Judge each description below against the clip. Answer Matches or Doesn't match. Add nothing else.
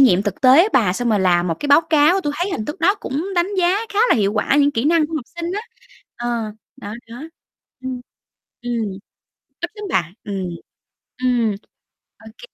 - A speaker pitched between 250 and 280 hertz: Matches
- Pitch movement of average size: Doesn't match